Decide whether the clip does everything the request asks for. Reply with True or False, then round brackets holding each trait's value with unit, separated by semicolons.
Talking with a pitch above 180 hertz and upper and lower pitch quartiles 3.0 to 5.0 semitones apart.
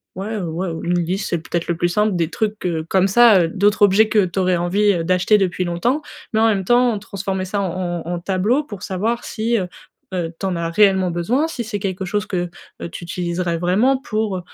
True (190 Hz; 3.3 semitones)